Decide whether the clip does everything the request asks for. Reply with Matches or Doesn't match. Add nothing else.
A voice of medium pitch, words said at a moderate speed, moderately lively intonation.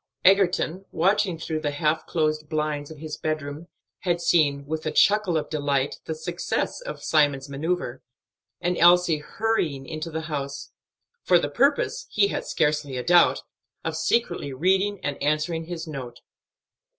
Matches